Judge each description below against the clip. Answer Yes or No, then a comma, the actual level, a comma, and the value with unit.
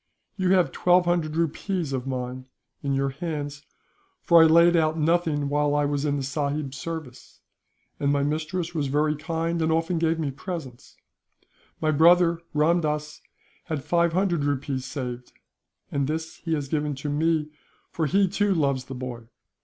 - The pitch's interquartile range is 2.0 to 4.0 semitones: Yes, average, 2.9 semitones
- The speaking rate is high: No, average, 165 wpm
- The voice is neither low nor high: Yes, medium, 155 Hz